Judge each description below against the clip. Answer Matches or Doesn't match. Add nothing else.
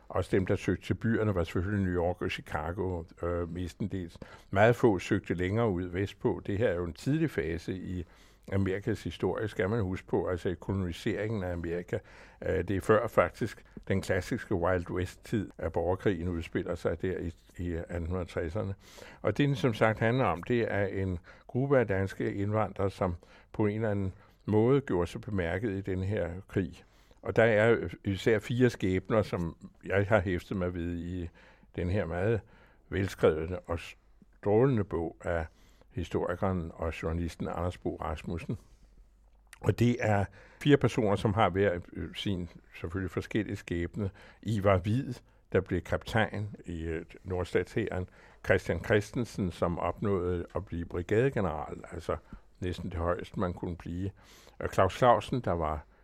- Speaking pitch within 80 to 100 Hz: Matches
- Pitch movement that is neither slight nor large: Matches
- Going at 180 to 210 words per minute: Doesn't match